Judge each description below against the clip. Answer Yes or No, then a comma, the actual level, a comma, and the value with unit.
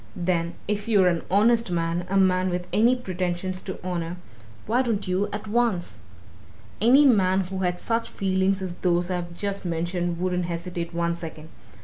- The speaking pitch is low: No, medium, 185 Hz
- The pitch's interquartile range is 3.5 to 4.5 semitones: No, narrow, 2.6 semitones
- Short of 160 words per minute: No, average, 165 wpm